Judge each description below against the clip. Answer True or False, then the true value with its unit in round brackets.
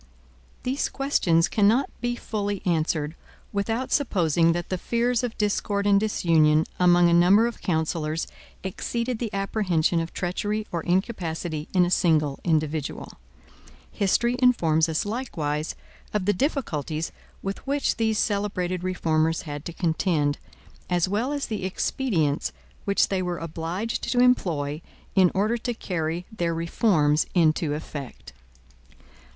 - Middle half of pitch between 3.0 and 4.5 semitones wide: False (5.0 semitones)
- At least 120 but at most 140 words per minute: True (135 wpm)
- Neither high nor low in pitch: True (180 Hz)